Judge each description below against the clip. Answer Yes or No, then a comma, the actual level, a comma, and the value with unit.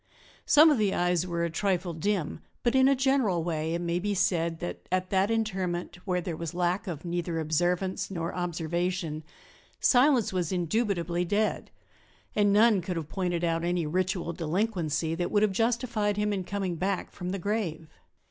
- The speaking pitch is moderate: Yes, medium, 180 Hz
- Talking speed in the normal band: Yes, average, 175 wpm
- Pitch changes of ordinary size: Yes, average, 3.3 semitones